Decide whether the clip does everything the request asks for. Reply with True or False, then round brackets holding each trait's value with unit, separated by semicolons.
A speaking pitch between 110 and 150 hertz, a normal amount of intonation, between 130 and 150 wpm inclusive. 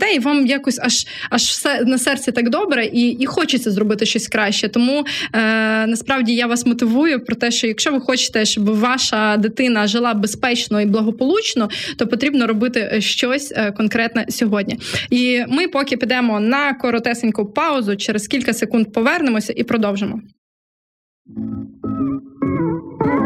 False (240 Hz; 3.1 semitones; 140 wpm)